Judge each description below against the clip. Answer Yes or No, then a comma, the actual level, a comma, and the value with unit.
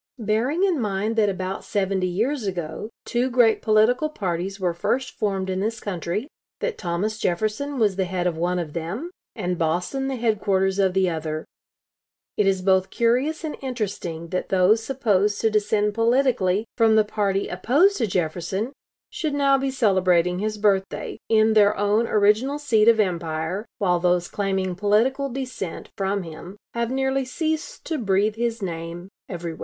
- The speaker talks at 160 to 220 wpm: Yes, average, 165 wpm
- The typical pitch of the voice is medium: No, high, 205 Hz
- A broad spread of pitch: No, average, 4.3 semitones